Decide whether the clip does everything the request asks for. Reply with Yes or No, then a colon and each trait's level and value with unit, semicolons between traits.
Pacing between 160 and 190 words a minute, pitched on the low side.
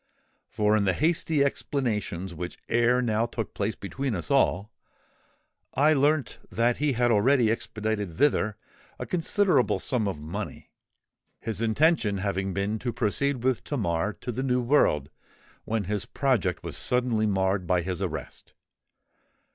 No: average, 145 wpm; low, 110 Hz